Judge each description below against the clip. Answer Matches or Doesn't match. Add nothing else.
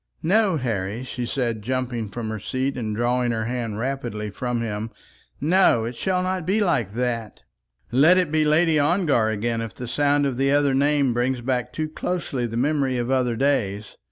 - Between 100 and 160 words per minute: Doesn't match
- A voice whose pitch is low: Matches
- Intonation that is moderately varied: Matches